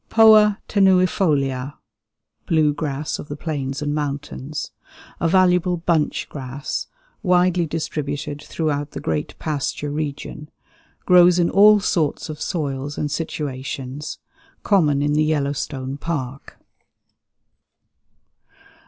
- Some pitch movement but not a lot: Yes, average, 3.5 semitones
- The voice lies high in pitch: No, medium, 150 Hz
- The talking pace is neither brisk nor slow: No, slow, 105 wpm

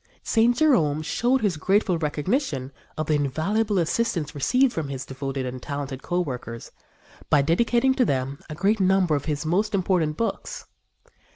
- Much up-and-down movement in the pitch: Yes, wide, 7.0 semitones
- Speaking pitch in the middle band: Yes, medium, 160 Hz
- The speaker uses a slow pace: No, average, 160 wpm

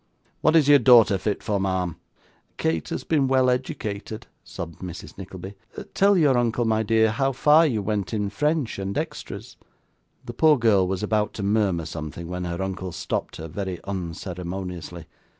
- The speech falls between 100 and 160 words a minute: No, average, 170 wpm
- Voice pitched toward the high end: No, low, 100 Hz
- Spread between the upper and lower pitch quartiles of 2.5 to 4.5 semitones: No, average, 5.0 semitones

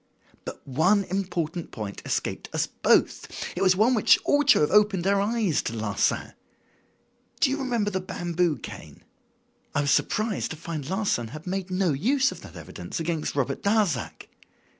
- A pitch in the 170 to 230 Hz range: Yes, medium, 185 Hz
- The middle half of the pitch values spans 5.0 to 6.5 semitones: Yes, average, 5.3 semitones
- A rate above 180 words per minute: No, average, 165 wpm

